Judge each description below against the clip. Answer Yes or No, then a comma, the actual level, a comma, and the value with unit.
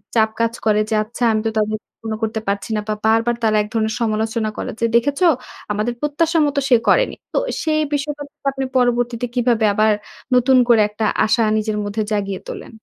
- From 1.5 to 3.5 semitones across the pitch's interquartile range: Yes, narrow, 2.6 semitones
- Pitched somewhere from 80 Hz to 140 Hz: No, high, 225 Hz